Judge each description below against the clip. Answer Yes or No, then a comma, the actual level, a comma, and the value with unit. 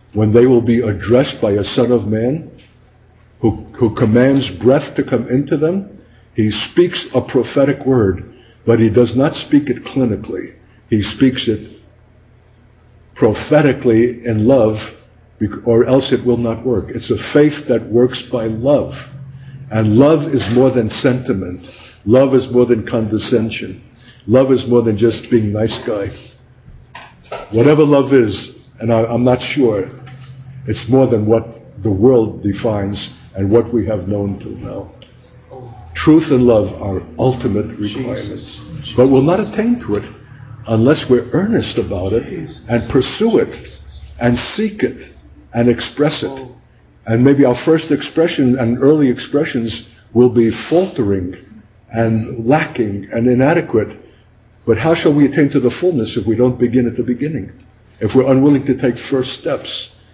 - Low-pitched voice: Yes, low, 120 Hz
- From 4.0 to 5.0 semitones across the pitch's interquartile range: No, average, 3.1 semitones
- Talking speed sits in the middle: Yes, average, 155 wpm